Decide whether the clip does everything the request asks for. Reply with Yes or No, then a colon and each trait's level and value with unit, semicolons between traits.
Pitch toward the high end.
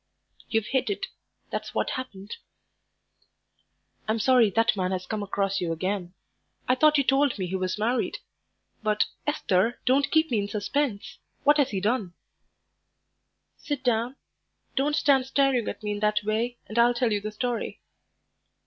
Yes: high, 225 Hz